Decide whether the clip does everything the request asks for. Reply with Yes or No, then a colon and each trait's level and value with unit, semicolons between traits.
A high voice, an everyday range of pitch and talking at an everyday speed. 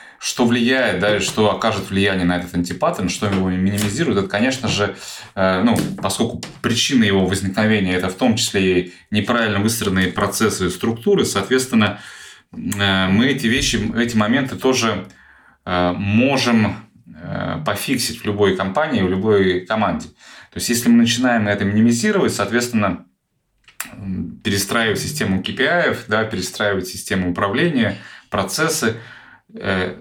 No: low, 105 Hz; average, 3.4 semitones; average, 120 wpm